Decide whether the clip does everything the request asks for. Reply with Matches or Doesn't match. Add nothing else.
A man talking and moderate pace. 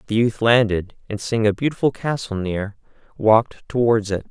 Matches